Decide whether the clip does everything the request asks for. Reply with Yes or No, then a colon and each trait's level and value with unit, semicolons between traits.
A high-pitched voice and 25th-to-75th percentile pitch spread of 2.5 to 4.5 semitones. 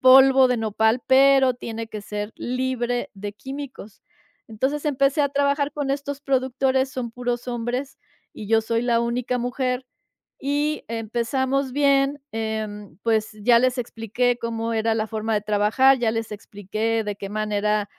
Yes: high, 240 Hz; average, 3.3 semitones